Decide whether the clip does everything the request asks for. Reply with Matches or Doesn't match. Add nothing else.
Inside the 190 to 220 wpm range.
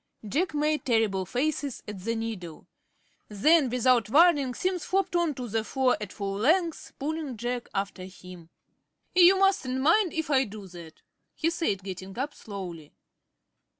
Doesn't match